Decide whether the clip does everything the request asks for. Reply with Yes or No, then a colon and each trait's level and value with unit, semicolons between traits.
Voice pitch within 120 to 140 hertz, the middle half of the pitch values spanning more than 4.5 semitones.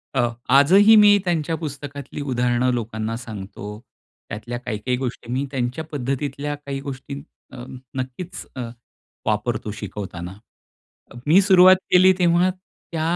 Yes: low, 135 Hz; average, 5.0 semitones